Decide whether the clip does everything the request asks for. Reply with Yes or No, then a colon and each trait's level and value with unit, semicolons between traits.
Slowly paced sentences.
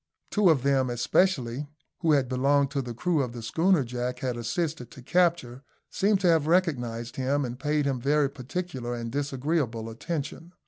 No: average, 175 wpm